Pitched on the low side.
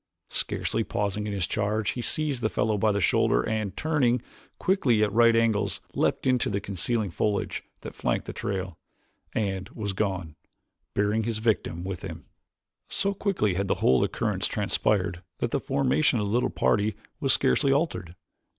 Yes: low, 105 Hz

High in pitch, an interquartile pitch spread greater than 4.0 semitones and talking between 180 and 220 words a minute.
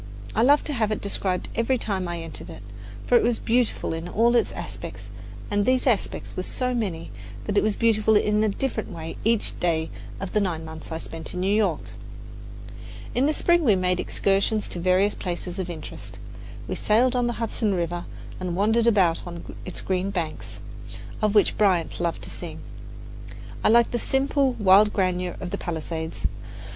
Yes: high, 200 Hz; average, 4.6 semitones; average, 185 wpm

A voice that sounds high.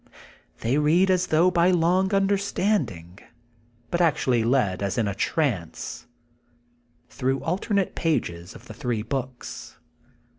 No: medium, 150 Hz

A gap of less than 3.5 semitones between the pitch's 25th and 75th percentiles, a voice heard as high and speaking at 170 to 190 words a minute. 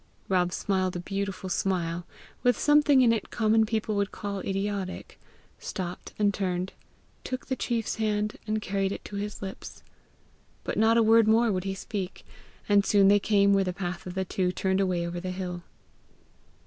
Yes: narrow, 2.6 semitones; high, 195 Hz; average, 180 wpm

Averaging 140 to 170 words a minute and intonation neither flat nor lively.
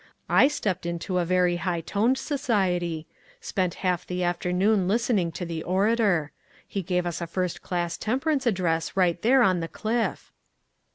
Yes: average, 160 wpm; average, 4.0 semitones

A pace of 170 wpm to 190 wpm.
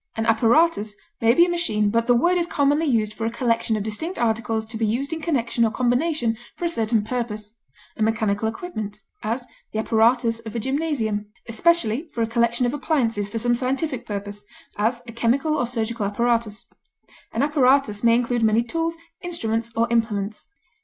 Yes: average, 180 wpm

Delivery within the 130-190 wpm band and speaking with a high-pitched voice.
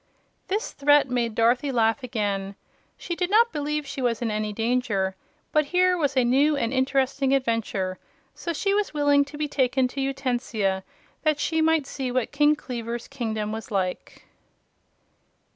Yes: average, 160 wpm; very high, 260 Hz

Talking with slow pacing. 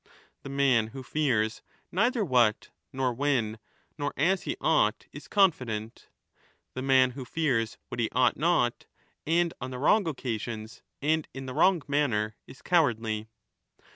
No: average, 145 wpm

